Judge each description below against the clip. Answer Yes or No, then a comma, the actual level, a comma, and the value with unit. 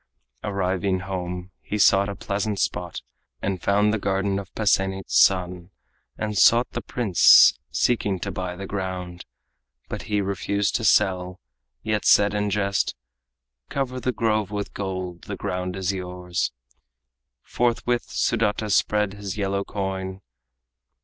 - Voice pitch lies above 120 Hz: No, low, 100 Hz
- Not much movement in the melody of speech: Yes, narrow, 2.0 semitones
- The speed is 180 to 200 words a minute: No, slow, 135 wpm